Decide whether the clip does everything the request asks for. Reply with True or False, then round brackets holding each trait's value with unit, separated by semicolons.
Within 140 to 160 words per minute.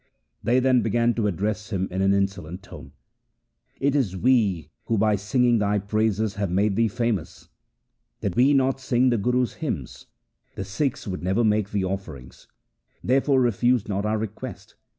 False (170 wpm)